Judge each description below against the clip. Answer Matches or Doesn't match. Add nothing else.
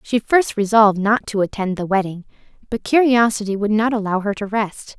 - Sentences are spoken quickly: Doesn't match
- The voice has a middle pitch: Doesn't match